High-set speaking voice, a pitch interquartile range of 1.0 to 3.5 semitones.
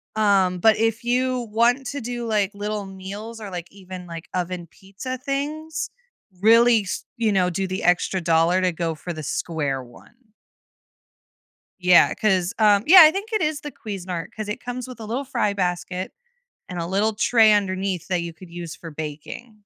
No: high, 200 Hz; average, 4.6 semitones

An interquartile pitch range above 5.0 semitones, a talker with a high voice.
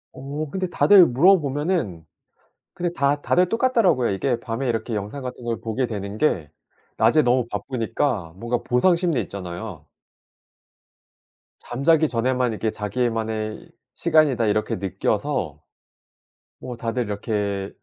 No: wide, 5.4 semitones; low, 120 Hz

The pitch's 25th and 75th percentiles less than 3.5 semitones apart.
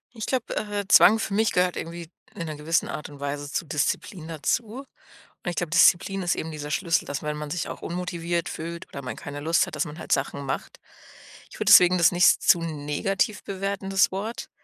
No: average, 4.2 semitones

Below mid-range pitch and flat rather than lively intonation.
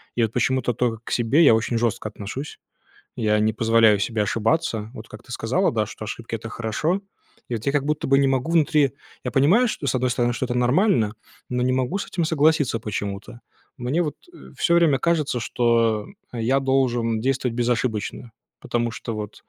No: low, 120 Hz; average, 3.5 semitones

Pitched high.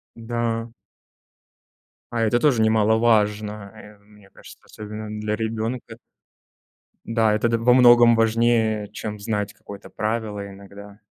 No: low, 110 Hz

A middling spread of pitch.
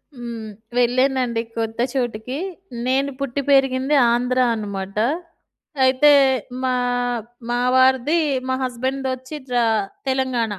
No: narrow, 1.9 semitones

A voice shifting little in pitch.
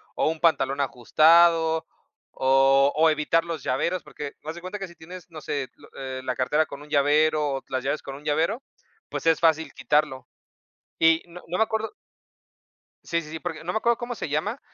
No: average, 3.2 semitones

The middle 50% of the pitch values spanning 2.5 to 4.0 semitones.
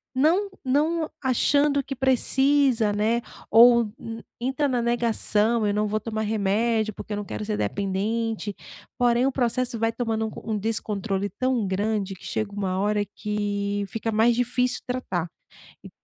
Yes: average, 3.2 semitones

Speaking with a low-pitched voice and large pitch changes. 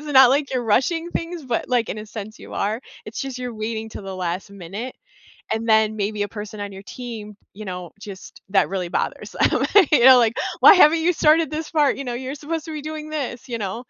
No: high, 235 Hz; wide, 5.8 semitones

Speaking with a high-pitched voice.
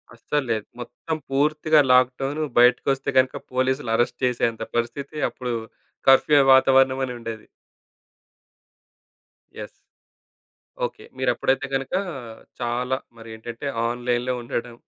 No: low, 125 Hz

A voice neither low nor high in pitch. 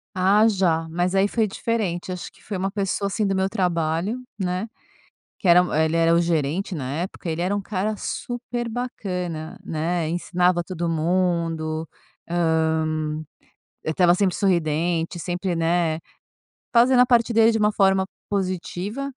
Yes: medium, 180 Hz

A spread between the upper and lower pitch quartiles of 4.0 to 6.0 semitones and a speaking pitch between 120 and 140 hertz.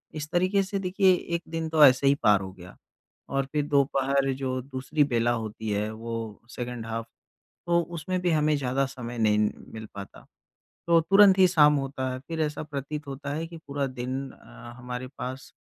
Yes: average, 4.5 semitones; low, 135 Hz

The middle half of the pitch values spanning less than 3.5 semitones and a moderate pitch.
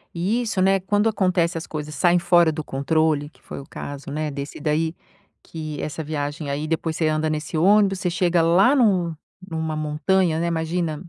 Yes: average, 2.8 semitones; medium, 160 Hz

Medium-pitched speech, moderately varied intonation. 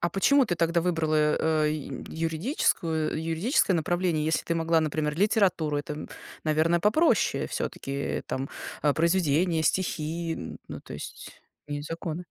No: medium, 160 Hz; narrow, 2.2 semitones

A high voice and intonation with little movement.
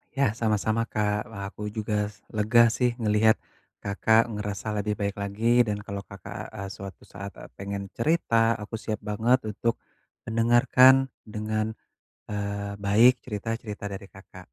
No: low, 105 Hz; narrow, 2.1 semitones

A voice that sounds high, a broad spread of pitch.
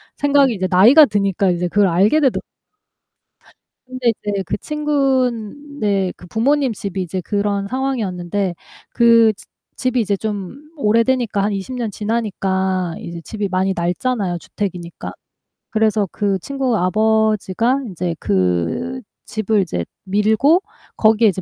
No: high, 210 Hz; average, 4.6 semitones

